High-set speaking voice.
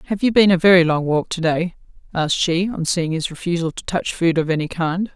No: medium, 170 Hz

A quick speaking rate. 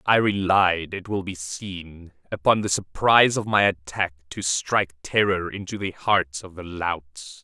No: average, 170 wpm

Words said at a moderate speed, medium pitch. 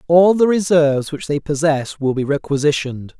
Yes: average, 170 wpm; medium, 150 Hz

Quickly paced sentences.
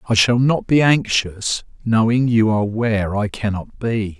No: average, 170 wpm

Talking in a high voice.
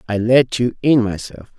No: low, 115 Hz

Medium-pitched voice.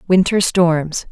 Yes: medium, 175 Hz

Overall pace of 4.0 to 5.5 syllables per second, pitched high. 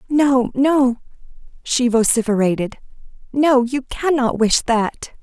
No: 3.7 syllables/s; very high, 250 Hz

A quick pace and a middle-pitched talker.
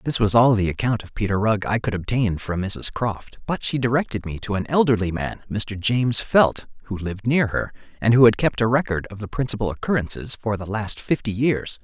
No: fast, 225 wpm; low, 110 Hz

